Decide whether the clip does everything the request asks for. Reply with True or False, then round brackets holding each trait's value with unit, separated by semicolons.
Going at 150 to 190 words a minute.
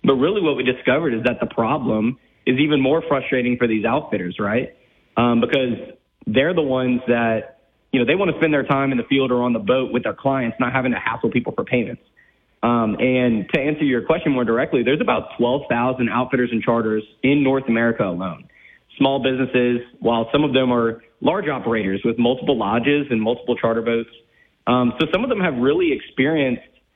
False (200 wpm)